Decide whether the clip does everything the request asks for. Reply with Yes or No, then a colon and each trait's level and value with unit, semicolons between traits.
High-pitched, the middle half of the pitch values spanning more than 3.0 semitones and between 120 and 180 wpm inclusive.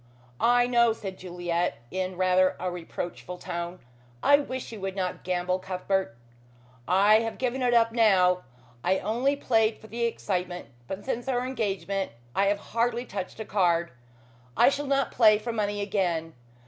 Yes: high, 200 Hz; average, 4.3 semitones; average, 160 wpm